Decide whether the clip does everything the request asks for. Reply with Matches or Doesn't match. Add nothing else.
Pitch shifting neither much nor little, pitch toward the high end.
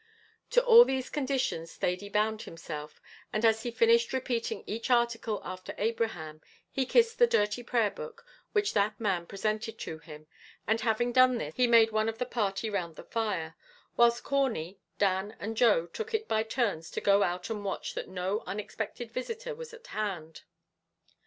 Matches